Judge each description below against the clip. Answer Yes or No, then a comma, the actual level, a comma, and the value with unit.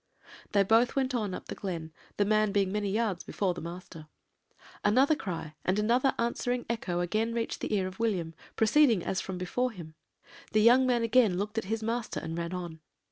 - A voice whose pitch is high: Yes, high, 210 Hz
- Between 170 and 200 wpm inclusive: Yes, average, 195 wpm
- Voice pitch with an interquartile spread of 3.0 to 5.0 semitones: Yes, average, 4.2 semitones